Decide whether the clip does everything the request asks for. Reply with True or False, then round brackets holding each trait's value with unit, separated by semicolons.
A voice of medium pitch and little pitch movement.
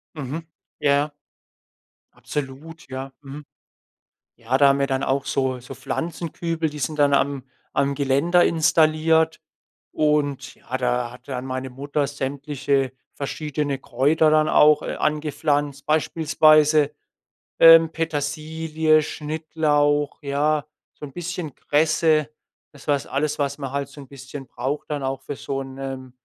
True (145 Hz; 2.2 semitones)